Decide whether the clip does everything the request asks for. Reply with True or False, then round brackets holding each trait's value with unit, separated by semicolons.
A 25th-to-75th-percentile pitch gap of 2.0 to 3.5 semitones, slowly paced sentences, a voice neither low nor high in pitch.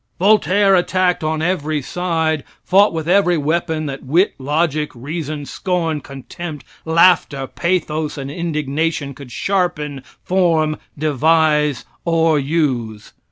True (3.0 semitones; 115 wpm; 155 Hz)